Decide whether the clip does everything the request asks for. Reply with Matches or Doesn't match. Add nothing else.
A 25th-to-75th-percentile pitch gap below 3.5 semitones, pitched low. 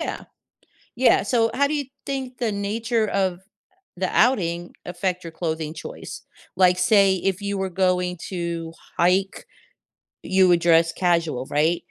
Doesn't match